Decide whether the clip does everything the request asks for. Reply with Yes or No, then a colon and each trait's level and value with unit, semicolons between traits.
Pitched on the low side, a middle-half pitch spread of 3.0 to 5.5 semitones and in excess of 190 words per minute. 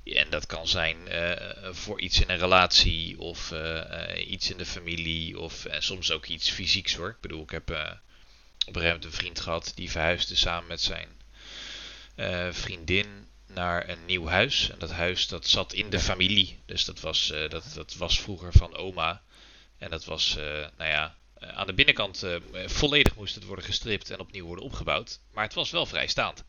No: very low, 90 Hz; narrow, 2.5 semitones; fast, 200 wpm